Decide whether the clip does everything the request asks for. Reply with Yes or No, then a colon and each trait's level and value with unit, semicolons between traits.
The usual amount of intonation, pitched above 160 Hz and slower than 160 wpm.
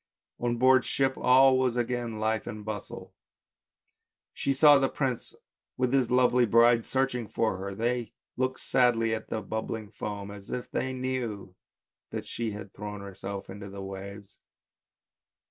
No: average, 3.7 semitones; low, 115 Hz; average, 150 wpm